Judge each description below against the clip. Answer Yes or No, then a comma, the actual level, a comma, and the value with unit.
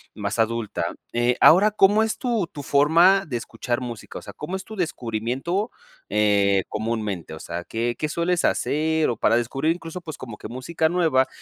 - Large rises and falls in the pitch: Yes, wide, 7.0 semitones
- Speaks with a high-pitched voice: No, low, 135 Hz